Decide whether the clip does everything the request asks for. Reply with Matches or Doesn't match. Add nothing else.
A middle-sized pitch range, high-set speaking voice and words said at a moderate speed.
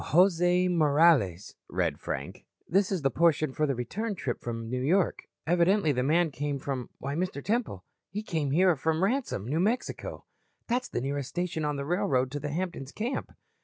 Doesn't match